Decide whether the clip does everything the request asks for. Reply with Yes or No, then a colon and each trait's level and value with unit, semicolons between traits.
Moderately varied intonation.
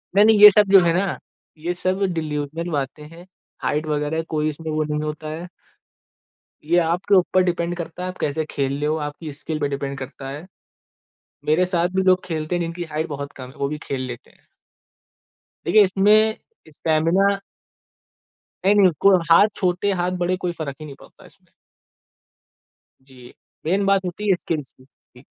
Yes: average, 3.7 semitones